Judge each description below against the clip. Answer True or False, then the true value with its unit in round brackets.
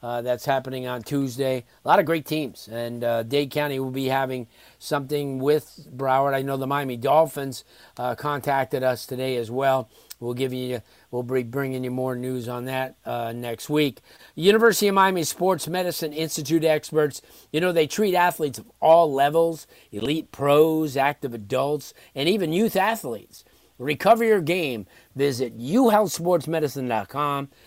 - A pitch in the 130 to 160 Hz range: True (140 Hz)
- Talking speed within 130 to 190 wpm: True (160 wpm)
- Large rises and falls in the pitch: False (3.8 semitones)